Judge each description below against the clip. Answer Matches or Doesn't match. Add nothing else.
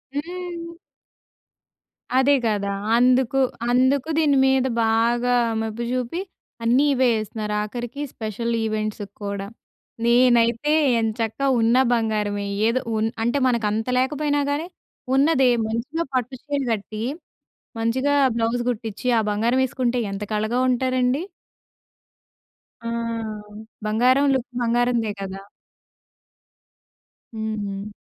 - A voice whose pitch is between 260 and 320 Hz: Doesn't match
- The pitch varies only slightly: Doesn't match